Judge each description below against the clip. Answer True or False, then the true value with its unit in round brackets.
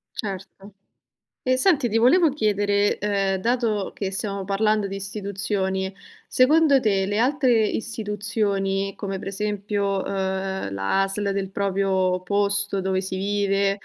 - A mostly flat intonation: True (1.6 semitones)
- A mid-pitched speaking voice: False (200 Hz)